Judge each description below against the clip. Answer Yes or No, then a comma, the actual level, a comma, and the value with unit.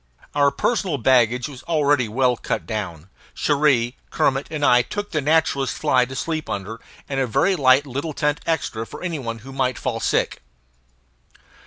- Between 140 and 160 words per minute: No, average, 170 wpm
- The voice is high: No, low, 135 Hz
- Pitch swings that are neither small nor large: Yes, average, 3.4 semitones